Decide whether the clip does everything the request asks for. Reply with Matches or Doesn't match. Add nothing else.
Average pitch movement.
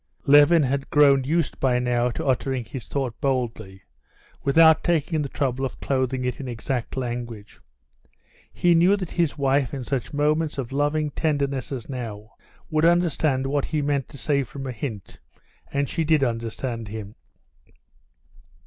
Matches